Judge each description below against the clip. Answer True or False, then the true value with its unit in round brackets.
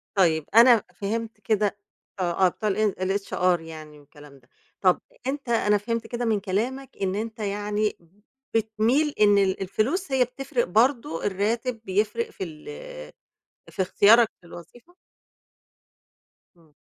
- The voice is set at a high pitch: True (210 Hz)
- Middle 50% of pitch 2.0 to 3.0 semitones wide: False (3.8 semitones)